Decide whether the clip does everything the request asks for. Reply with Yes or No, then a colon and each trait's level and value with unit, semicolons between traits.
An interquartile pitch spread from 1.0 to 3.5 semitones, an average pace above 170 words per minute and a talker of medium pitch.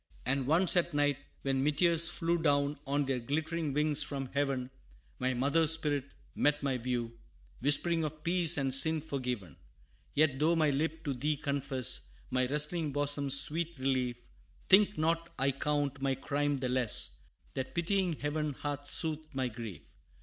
No: average, 2.9 semitones; average, 155 wpm; medium, 145 Hz